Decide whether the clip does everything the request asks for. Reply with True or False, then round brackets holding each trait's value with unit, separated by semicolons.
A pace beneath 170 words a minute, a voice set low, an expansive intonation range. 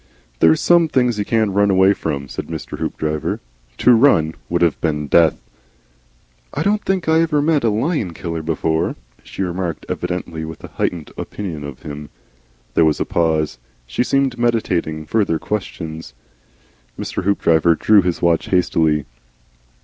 True (155 wpm; 85 Hz; 6.0 semitones)